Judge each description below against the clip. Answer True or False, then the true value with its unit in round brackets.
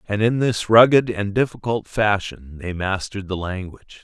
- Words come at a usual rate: True (165 wpm)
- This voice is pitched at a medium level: False (105 Hz)